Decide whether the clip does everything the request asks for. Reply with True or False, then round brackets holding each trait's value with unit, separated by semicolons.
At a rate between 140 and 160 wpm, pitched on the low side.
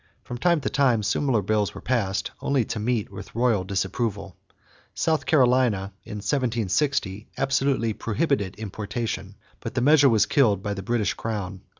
True (155 wpm; 115 Hz)